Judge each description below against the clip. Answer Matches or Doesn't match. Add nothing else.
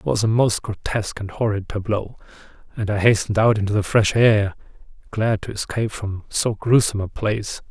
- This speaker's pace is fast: Doesn't match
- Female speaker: Doesn't match